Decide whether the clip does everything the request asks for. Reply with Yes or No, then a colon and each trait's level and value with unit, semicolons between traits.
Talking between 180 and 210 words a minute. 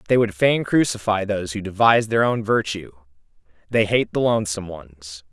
No: average, 160 wpm